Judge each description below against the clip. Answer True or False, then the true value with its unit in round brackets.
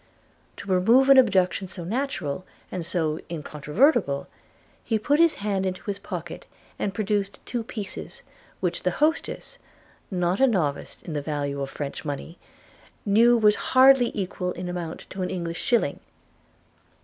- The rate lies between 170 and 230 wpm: False (150 wpm)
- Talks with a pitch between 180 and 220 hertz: True (190 Hz)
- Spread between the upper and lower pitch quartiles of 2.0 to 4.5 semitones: False (5.4 semitones)